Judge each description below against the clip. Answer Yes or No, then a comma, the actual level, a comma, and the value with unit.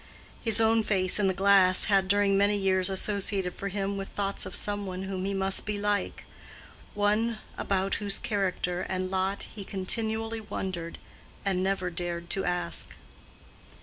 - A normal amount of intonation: No, narrow, 1.7 semitones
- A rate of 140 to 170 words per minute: Yes, average, 155 wpm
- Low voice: No, high, 195 Hz